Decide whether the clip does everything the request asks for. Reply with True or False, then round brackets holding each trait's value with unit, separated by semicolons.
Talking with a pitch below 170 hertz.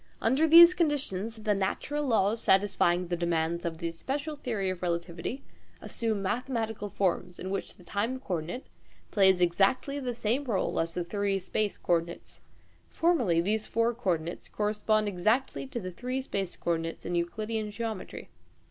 False (205 Hz)